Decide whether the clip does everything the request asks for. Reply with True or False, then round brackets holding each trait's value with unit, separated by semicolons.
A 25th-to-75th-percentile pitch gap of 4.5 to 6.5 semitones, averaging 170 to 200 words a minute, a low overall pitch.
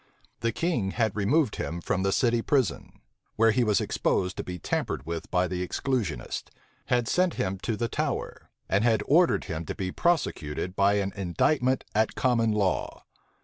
True (4.9 semitones; 175 wpm; 105 Hz)